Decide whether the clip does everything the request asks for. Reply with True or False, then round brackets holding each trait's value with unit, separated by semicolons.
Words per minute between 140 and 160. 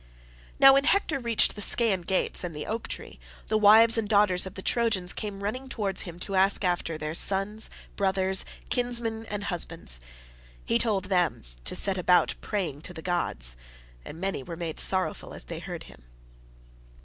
False (175 wpm)